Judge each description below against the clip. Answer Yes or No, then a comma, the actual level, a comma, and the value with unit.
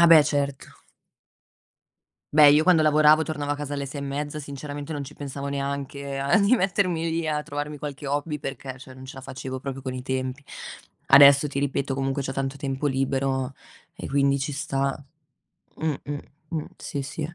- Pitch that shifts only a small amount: Yes, narrow, 1.7 semitones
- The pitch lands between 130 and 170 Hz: Yes, medium, 140 Hz